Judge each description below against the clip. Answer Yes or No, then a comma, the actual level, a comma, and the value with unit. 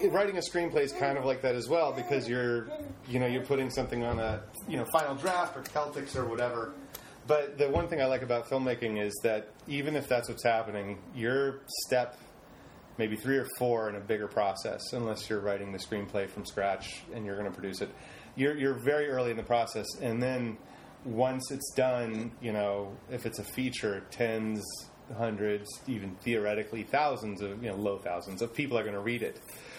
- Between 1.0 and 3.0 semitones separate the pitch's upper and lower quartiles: No, average, 4.0 semitones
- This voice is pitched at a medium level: No, low, 120 Hz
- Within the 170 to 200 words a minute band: Yes, average, 195 wpm